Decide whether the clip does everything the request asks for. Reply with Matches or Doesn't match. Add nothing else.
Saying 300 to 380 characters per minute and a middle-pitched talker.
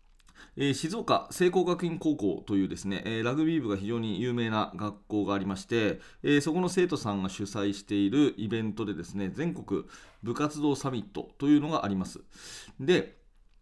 Doesn't match